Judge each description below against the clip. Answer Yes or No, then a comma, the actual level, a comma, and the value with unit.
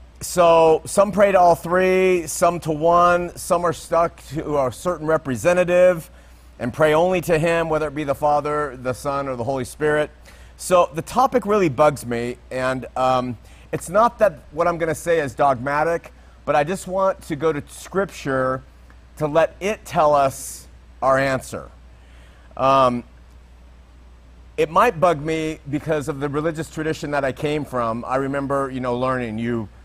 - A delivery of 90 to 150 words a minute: No, fast, 170 wpm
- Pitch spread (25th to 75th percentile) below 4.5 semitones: No, average, 5.2 semitones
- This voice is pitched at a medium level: Yes, medium, 150 Hz